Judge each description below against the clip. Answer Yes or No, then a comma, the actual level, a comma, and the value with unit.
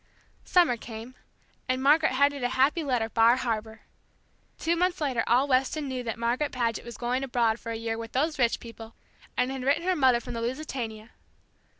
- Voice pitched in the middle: No, very high, 250 Hz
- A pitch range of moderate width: Yes, average, 3.4 semitones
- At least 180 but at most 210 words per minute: Yes, average, 190 wpm